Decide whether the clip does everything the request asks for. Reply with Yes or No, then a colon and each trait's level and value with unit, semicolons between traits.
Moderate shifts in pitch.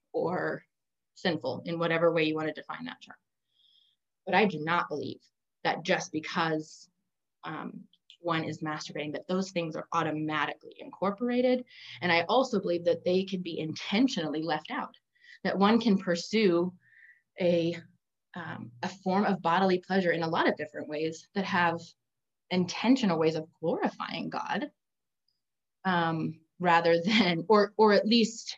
Yes: average, 3.5 semitones